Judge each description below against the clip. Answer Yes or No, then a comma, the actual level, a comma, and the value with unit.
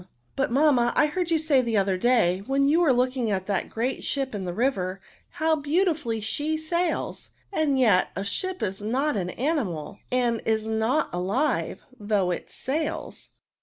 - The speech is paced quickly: No, average, 185 wpm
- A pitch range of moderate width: No, wide, 6.6 semitones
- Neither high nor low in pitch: No, very high, 250 Hz